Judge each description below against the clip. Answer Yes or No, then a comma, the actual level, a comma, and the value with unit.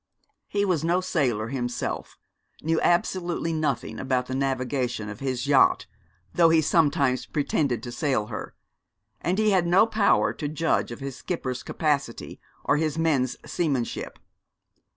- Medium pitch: Yes, medium, 145 Hz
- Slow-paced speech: No, average, 145 wpm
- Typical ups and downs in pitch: Yes, average, 4.5 semitones